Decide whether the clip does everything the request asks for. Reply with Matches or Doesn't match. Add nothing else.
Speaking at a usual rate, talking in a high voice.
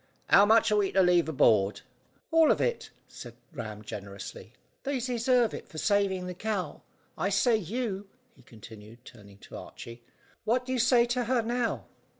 Matches